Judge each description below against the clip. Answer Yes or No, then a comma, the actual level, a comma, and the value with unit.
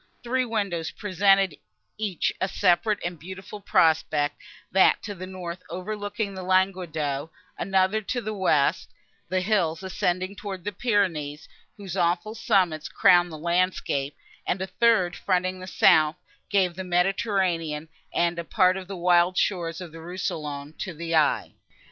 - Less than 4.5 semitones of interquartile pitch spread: Yes, average, 2.7 semitones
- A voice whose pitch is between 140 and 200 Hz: Yes, medium, 185 Hz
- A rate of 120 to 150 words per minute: Yes, average, 140 wpm